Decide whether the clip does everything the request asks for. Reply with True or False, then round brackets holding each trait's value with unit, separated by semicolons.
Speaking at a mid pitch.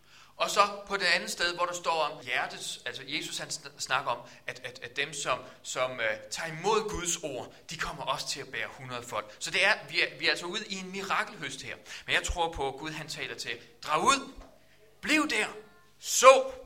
True (160 Hz)